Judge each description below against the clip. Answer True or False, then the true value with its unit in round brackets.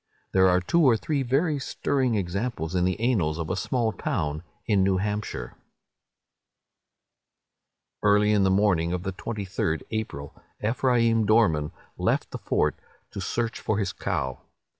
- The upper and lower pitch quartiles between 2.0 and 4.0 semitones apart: False (4.4 semitones)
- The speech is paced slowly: False (145 wpm)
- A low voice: True (105 Hz)